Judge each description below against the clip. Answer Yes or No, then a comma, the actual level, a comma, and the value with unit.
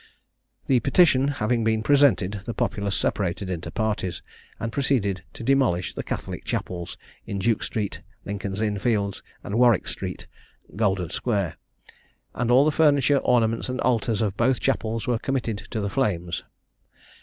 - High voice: No, low, 110 Hz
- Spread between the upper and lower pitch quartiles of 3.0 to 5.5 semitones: Yes, average, 4.1 semitones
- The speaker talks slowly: No, average, 150 wpm